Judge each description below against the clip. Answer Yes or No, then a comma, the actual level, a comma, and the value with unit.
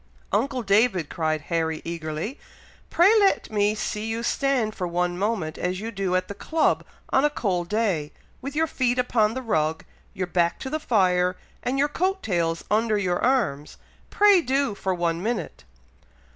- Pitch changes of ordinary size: No, wide, 6.1 semitones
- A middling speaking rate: Yes, average, 170 wpm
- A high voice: Yes, high, 205 Hz